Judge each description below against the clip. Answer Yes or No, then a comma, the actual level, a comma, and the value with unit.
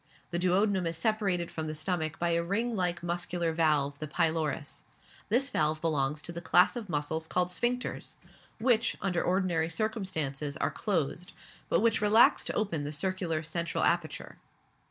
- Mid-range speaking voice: Yes, medium, 170 Hz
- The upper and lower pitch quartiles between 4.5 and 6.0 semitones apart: No, average, 3.6 semitones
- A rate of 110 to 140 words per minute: No, average, 160 wpm